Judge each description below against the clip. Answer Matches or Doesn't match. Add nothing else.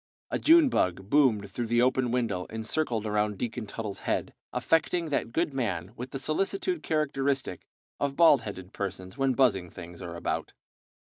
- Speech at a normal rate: Matches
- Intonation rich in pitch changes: Matches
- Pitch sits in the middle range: Doesn't match